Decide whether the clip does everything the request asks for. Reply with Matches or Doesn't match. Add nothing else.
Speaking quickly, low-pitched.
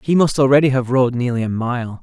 Matches